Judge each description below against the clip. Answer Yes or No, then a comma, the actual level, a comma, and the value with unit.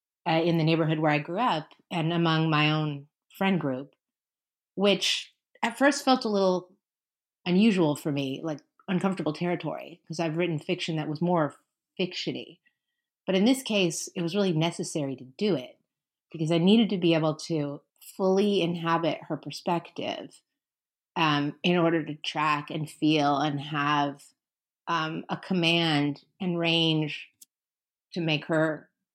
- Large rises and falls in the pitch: No, average, 3.3 semitones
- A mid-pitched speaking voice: Yes, medium, 165 Hz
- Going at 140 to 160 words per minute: Yes, average, 150 wpm